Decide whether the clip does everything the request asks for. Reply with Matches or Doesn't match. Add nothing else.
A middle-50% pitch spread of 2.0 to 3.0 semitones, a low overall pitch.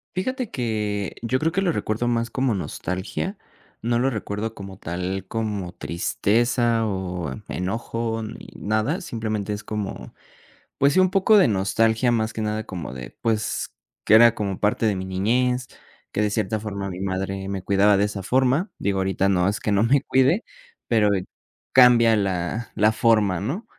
Doesn't match